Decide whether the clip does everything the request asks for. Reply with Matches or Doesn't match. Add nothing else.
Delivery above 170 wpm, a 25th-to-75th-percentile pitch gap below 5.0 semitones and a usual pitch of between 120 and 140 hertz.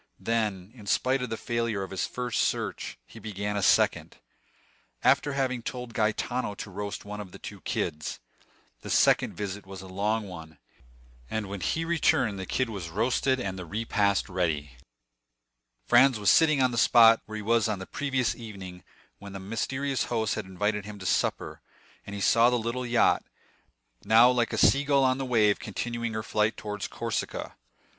Doesn't match